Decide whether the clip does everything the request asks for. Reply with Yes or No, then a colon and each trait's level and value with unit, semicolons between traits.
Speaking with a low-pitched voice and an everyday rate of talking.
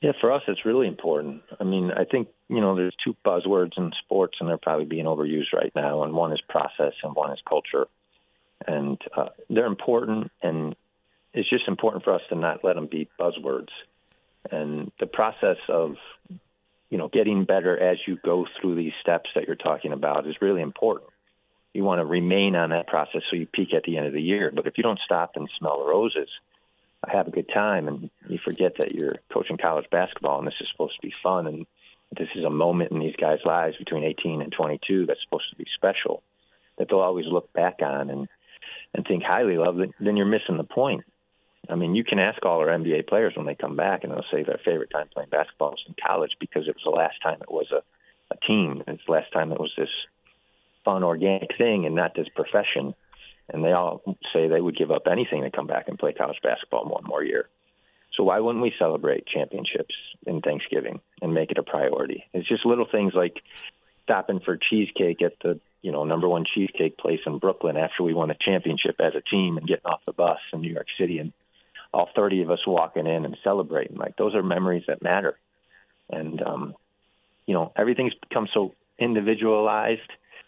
No: low, 100 Hz; fast, 215 wpm